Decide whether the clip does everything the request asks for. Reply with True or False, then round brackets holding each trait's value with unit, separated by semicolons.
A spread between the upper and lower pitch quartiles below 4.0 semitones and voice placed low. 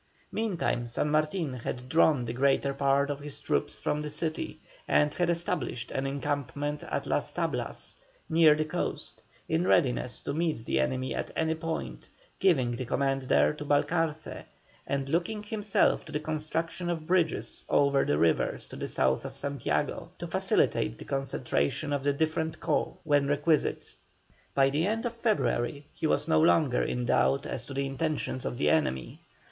False (3.2 semitones; 145 Hz)